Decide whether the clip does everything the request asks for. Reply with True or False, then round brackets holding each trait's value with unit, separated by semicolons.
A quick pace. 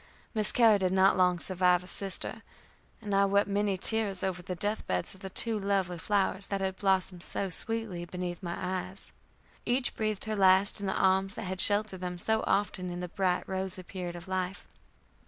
False (195 wpm)